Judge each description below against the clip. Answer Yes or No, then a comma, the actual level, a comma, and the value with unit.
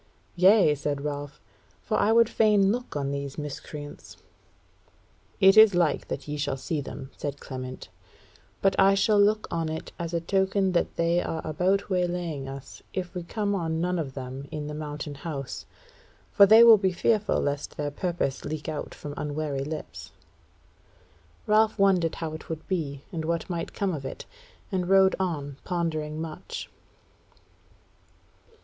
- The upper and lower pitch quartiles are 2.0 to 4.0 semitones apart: No, average, 4.7 semitones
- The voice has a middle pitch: Yes, medium, 165 Hz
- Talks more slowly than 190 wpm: Yes, average, 160 wpm